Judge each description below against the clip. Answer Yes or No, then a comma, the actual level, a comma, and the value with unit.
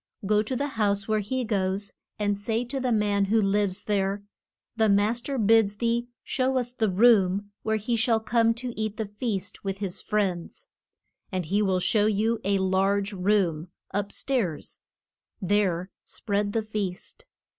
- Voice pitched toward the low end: No, high, 205 Hz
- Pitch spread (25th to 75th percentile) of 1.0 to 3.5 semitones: Yes, narrow, 2.5 semitones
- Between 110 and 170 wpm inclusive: Yes, average, 165 wpm